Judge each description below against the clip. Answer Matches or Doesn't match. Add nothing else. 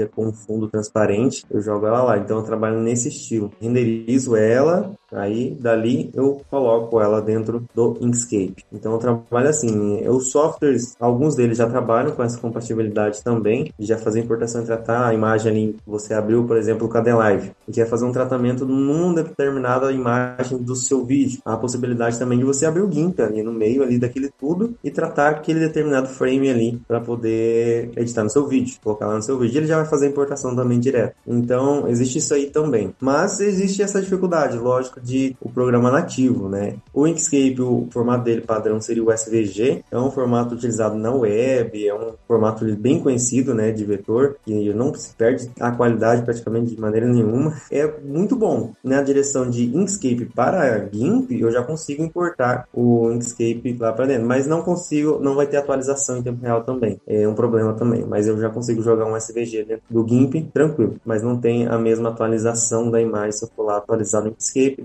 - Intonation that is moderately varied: Matches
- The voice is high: Doesn't match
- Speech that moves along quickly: Matches